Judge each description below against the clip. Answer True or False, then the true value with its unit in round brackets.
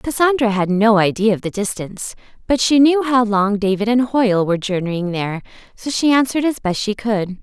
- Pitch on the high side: True (220 Hz)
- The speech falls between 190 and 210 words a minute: True (200 wpm)